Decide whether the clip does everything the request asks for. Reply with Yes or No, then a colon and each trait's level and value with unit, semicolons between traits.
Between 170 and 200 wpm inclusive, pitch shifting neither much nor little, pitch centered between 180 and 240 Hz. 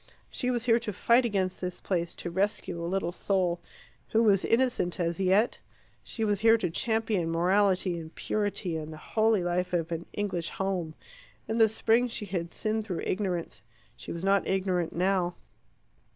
Yes: average, 175 wpm; average, 3.8 semitones; high, 190 Hz